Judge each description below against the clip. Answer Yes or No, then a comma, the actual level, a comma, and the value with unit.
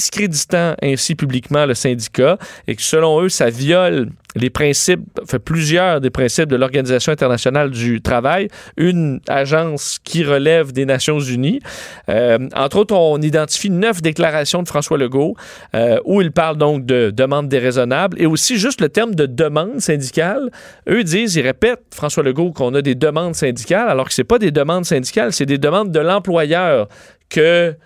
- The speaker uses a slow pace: No, average, 170 wpm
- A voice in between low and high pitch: Yes, medium, 155 Hz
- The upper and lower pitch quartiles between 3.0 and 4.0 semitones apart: No, average, 4.4 semitones